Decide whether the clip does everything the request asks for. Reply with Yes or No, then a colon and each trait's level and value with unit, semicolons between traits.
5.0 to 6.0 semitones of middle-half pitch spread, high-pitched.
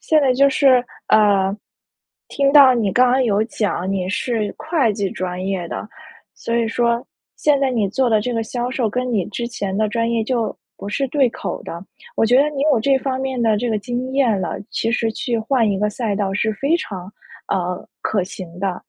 No: average, 4.1 semitones; high, 230 Hz